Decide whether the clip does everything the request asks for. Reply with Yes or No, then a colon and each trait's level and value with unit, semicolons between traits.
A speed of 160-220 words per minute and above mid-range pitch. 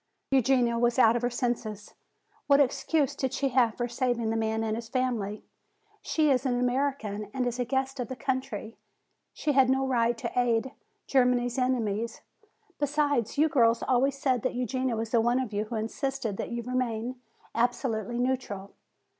Yes: average, 175 wpm; high, 245 Hz